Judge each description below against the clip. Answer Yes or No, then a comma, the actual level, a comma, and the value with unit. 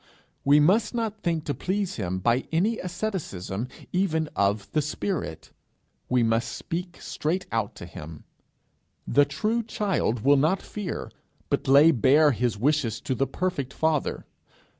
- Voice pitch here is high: No, medium, 150 Hz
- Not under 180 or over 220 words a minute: No, average, 145 wpm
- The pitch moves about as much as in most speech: No, wide, 7.6 semitones